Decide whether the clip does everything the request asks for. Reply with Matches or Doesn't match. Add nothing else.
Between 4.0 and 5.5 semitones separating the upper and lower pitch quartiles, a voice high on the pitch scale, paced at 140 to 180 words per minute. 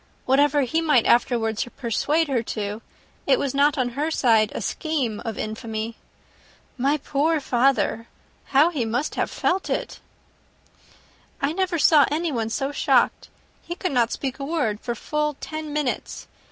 Matches